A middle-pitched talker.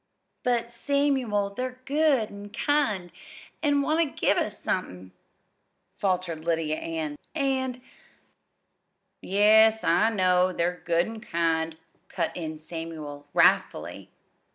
No: high, 200 Hz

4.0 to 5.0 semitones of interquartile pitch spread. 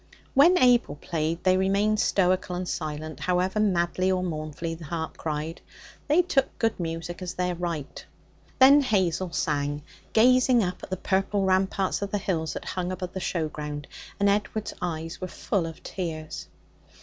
No: average, 3.5 semitones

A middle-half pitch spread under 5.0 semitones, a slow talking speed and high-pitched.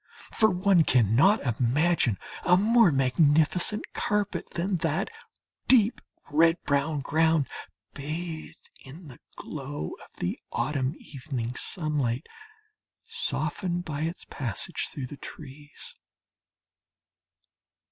No: average, 4.5 semitones; slow, 100 wpm; medium, 155 Hz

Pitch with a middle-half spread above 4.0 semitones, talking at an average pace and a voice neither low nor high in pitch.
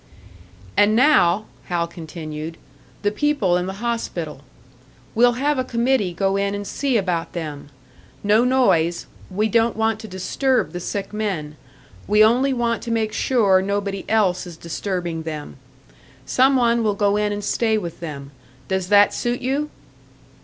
No: average, 4.9 semitones; average, 155 wpm; high, 205 Hz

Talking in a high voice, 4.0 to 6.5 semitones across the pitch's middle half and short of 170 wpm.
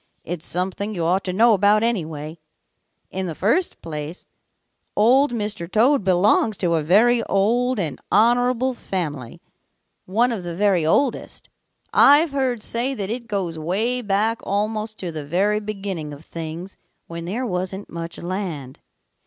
Yes: high, 200 Hz; average, 5.1 semitones; average, 150 wpm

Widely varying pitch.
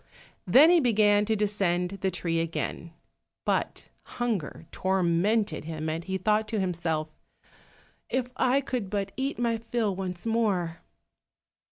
No: average, 4.7 semitones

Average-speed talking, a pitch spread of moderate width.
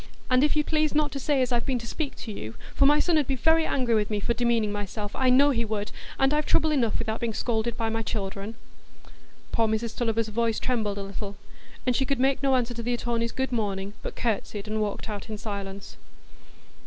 No: fast, 230 wpm; average, 3.7 semitones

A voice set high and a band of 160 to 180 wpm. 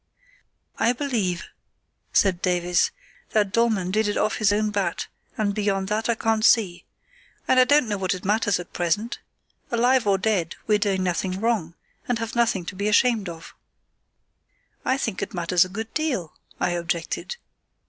Yes: high, 205 Hz; average, 170 wpm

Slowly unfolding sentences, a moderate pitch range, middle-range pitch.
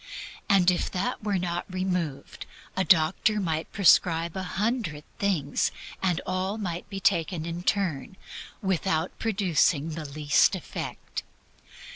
Yes: slow, 120 wpm; average, 3.1 semitones; medium, 180 Hz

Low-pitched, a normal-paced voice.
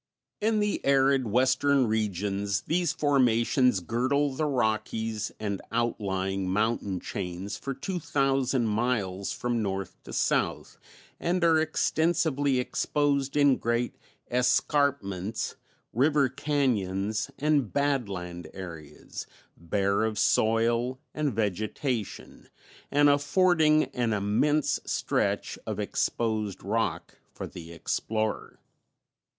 No: low, 120 Hz; slow, 100 wpm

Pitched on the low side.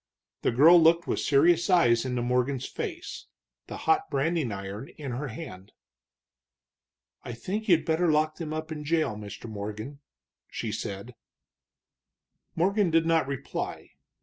No: medium, 150 Hz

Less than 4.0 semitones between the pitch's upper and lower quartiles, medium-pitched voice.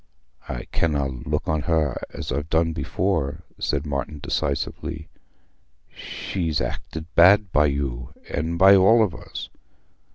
No: average, 2.9 semitones; very low, 80 Hz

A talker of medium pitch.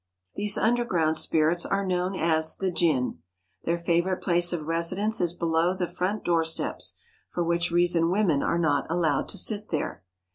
Yes: medium, 170 Hz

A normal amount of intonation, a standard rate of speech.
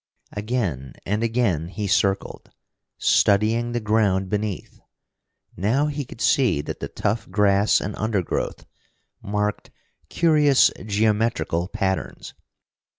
No: average, 3.0 semitones; slow, 105 wpm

